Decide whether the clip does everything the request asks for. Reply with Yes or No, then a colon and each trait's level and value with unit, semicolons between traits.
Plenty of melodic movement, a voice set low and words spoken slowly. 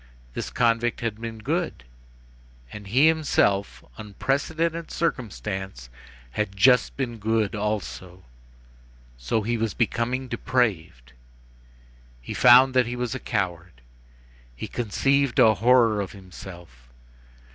No: average, 4.5 semitones; low, 110 Hz; slow, 115 wpm